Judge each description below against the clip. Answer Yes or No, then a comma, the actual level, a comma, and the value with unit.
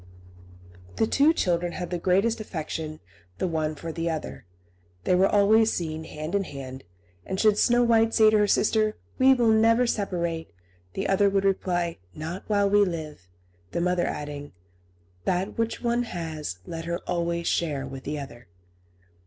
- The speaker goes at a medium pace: Yes, average, 165 wpm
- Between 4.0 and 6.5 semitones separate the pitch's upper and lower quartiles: Yes, average, 5.1 semitones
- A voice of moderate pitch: Yes, medium, 180 Hz